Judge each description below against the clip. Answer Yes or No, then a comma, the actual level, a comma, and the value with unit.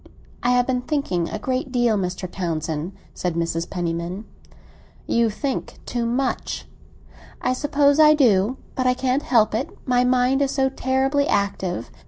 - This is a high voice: Yes, high, 245 Hz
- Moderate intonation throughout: No, wide, 6.1 semitones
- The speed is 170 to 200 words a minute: No, average, 155 wpm